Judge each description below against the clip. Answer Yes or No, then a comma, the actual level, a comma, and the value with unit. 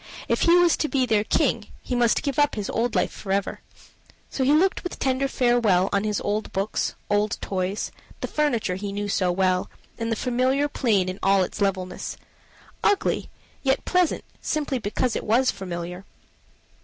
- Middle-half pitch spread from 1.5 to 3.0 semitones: No, wide, 5.4 semitones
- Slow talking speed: No, average, 175 wpm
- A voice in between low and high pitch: No, high, 220 Hz